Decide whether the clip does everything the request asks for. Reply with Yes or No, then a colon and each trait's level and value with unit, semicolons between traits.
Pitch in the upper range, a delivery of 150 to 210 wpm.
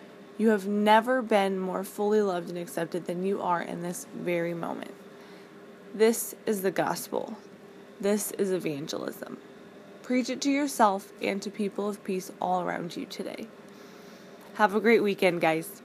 Yes: high, 205 Hz; average, 155 wpm